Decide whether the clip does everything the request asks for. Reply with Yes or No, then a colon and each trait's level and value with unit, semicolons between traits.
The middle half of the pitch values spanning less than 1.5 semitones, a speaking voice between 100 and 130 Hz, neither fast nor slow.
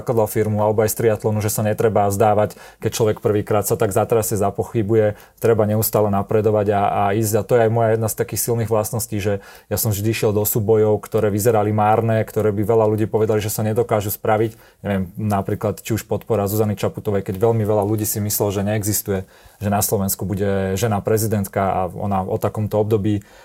No: narrow, 1.1 semitones; low, 105 Hz; fast, 200 wpm